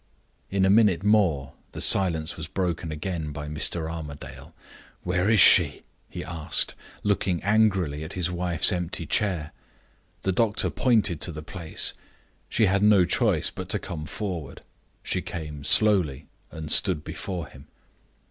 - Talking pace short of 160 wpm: Yes, average, 145 wpm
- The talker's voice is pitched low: Yes, very low, 85 Hz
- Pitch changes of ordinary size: Yes, average, 3.9 semitones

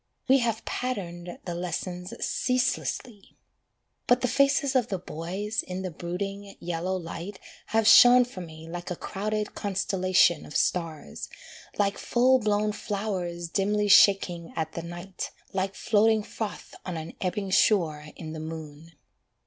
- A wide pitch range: No, average, 3.6 semitones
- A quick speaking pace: No, average, 140 wpm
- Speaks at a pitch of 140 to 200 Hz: Yes, high, 190 Hz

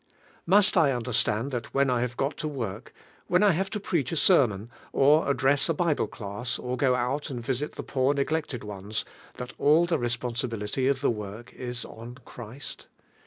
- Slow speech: No, average, 195 wpm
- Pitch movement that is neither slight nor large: Yes, average, 3.8 semitones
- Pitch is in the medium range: No, low, 130 Hz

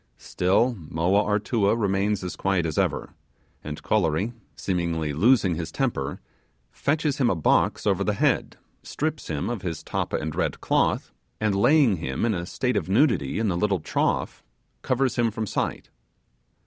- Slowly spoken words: No, average, 160 wpm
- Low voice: Yes, low, 100 Hz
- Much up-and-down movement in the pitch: Yes, wide, 5.7 semitones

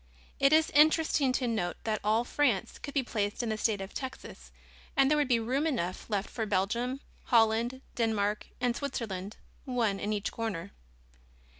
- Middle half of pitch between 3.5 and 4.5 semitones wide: Yes, average, 4.1 semitones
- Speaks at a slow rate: No, average, 170 wpm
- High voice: Yes, high, 230 Hz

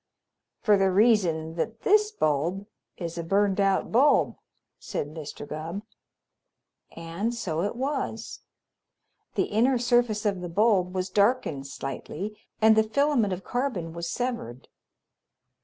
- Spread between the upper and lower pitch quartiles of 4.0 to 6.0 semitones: Yes, wide, 5.6 semitones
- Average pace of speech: No, slow, 130 wpm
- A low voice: No, high, 200 Hz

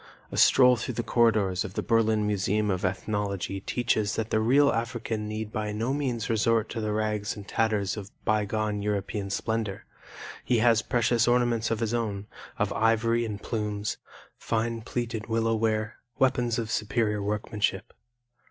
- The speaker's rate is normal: Yes, average, 160 wpm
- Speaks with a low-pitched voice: Yes, low, 110 Hz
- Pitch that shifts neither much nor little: No, narrow, 1.7 semitones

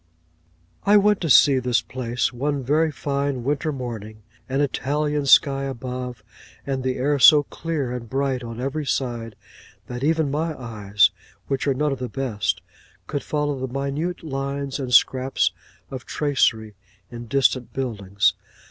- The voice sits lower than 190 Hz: Yes, low, 135 Hz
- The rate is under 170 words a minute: Yes, average, 150 wpm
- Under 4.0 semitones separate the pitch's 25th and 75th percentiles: Yes, average, 2.8 semitones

